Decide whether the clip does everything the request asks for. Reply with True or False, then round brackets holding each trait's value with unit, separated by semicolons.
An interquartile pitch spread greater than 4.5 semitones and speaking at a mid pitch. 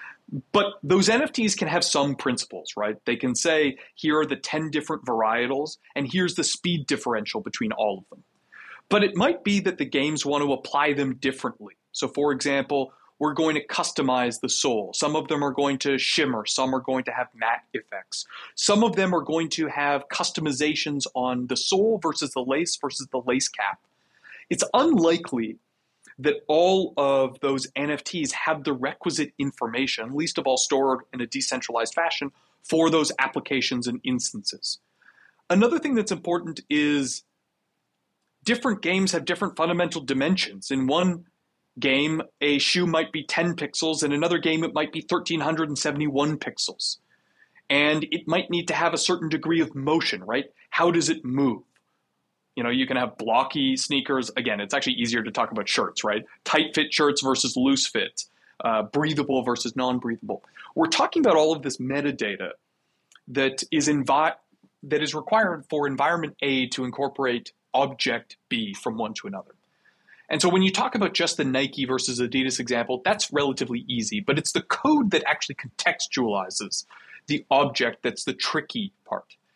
False (4.0 semitones; 150 Hz)